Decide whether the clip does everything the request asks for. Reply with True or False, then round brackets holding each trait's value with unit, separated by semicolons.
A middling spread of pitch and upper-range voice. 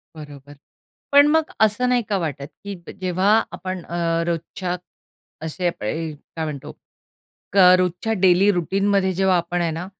False (3.3 semitones; 180 Hz)